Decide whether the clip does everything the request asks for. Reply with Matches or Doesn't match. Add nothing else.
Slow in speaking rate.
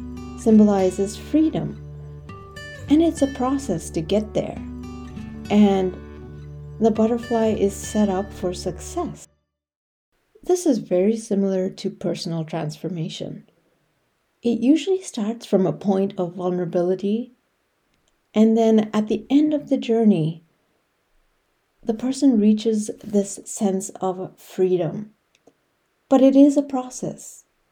Matches